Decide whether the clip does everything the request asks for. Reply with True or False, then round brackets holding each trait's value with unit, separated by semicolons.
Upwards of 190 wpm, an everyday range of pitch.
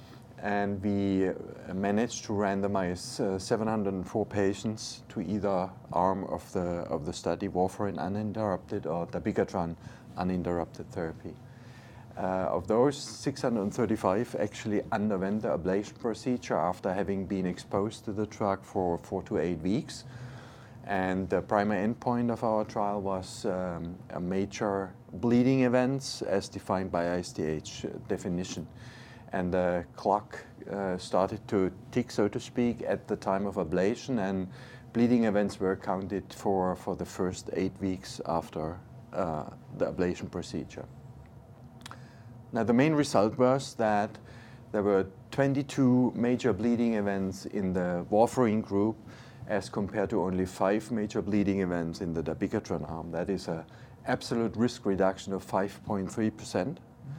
False (135 wpm; 4.2 semitones)